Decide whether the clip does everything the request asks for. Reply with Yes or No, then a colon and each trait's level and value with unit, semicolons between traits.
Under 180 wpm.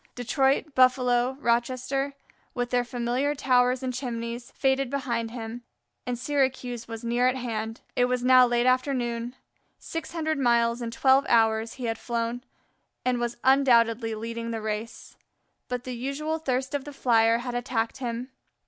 Yes: average, 155 wpm